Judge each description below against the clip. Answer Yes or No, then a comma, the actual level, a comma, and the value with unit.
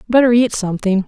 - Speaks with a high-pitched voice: Yes, high, 215 Hz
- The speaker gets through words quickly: No, average, 170 wpm